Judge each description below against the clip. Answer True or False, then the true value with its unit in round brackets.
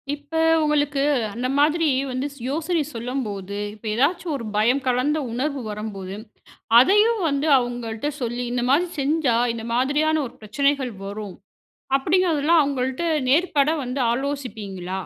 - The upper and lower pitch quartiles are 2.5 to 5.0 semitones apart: True (4.3 semitones)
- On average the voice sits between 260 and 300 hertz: True (265 Hz)